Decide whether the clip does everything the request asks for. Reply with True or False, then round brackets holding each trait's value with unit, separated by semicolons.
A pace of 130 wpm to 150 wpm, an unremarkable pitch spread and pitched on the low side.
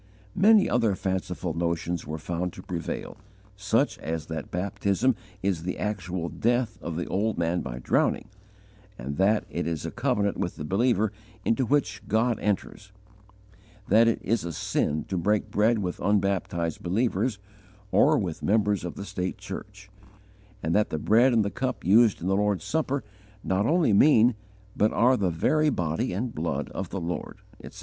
False (170 wpm; 4.5 semitones; 100 Hz)